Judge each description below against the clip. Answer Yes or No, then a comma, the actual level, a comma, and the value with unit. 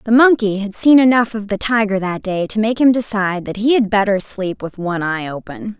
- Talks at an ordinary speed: No, fast, 240 wpm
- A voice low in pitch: No, high, 210 Hz